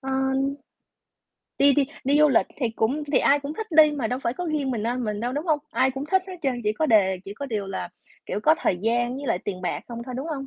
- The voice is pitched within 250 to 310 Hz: Yes, very high, 265 Hz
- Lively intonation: No, average, 4.3 semitones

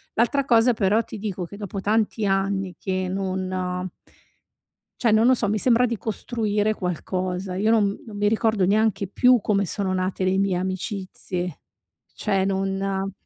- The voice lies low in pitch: No, high, 195 Hz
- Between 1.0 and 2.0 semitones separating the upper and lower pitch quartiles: No, narrow, 2.6 semitones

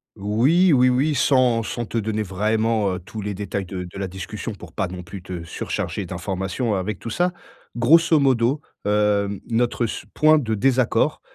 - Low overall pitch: Yes, low, 110 Hz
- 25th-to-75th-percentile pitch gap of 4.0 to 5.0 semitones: Yes, average, 4.5 semitones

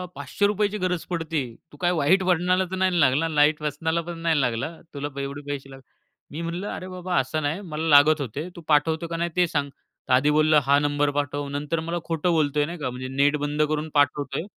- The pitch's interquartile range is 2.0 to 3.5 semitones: Yes, average, 3.0 semitones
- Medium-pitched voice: Yes, medium, 155 Hz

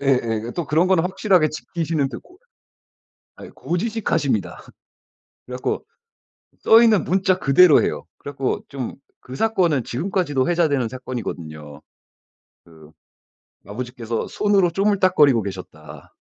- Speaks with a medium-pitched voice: Yes, medium, 145 Hz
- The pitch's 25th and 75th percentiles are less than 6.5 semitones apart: No, wide, 7.0 semitones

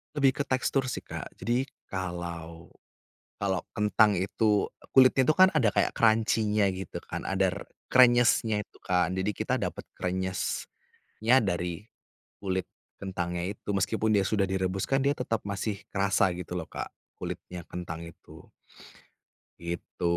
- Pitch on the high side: No, low, 100 Hz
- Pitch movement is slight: No, average, 3.7 semitones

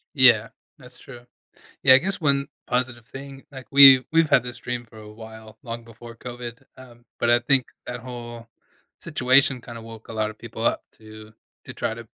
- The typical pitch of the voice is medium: No, low, 120 Hz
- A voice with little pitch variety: Yes, narrow, 2.2 semitones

